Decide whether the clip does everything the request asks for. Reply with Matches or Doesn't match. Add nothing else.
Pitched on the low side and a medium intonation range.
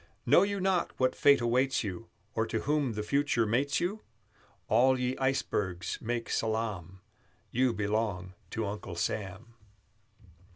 Matches